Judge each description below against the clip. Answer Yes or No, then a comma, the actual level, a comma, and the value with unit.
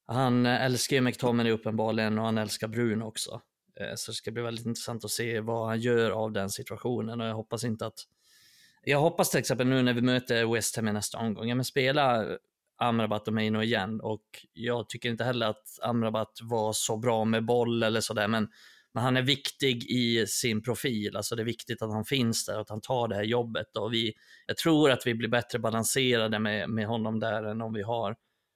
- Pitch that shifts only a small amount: Yes, narrow, 1.8 semitones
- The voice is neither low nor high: No, low, 115 Hz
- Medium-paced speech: No, fast, 220 wpm